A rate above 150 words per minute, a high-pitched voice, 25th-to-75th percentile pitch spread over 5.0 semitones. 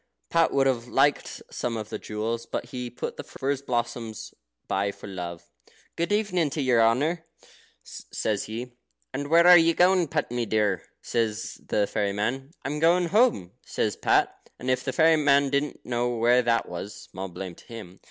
No: average, 180 wpm; low, 120 Hz; wide, 5.4 semitones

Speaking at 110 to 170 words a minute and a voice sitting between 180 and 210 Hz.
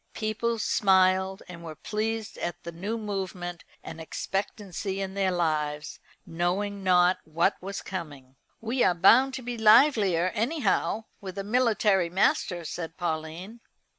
Yes: slow, 135 wpm; high, 190 Hz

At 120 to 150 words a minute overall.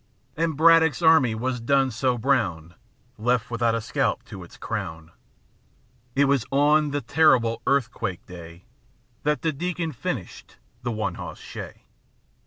Yes: average, 140 wpm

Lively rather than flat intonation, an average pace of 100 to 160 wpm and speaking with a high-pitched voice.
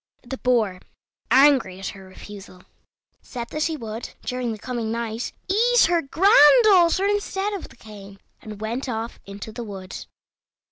Yes: wide, 7.3 semitones; average, 150 wpm; high, 240 Hz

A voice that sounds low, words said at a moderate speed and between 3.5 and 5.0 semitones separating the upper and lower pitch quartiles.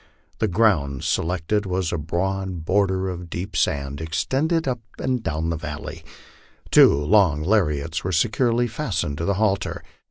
Yes: very low, 90 Hz; average, 150 wpm; average, 4.7 semitones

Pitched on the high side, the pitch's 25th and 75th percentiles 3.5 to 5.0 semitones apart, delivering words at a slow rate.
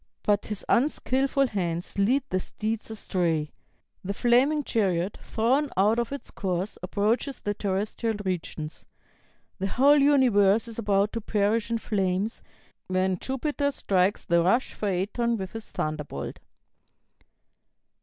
Yes: high, 210 Hz; average, 4.2 semitones; slow, 125 wpm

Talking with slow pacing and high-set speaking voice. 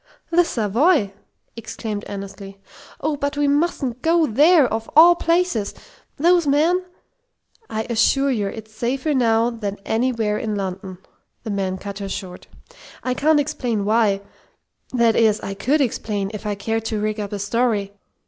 No: average, 160 wpm; high, 225 Hz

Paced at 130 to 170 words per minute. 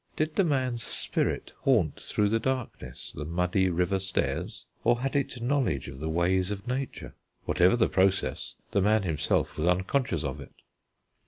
Yes: average, 165 wpm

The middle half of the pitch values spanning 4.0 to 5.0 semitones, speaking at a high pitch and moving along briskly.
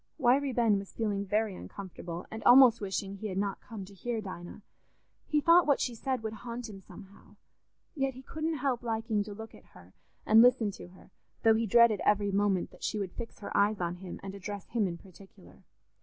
No: average, 3.4 semitones; high, 215 Hz; fast, 210 wpm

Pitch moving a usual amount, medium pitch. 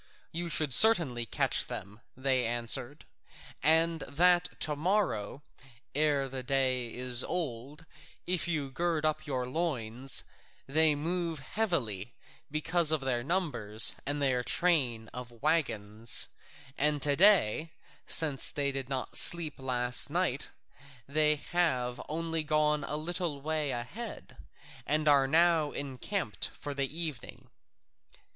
Yes: average, 4.3 semitones; medium, 145 Hz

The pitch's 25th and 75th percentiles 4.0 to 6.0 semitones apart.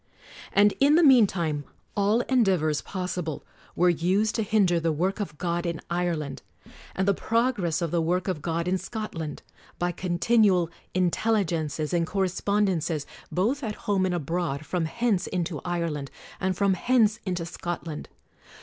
No: average, 3.5 semitones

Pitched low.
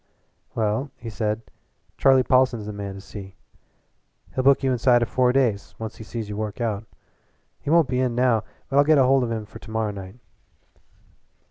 Yes: low, 115 Hz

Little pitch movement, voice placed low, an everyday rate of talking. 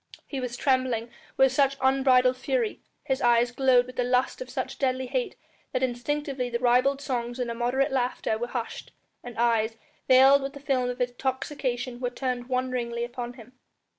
No: narrow, 1.6 semitones; very high, 255 Hz; average, 170 wpm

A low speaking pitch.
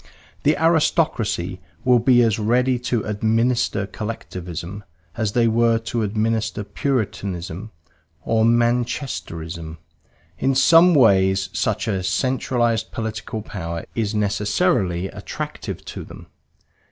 Yes: low, 110 Hz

